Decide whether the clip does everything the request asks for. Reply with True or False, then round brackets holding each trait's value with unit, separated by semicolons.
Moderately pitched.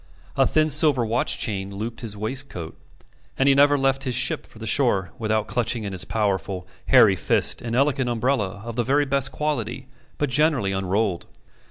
False (120 Hz)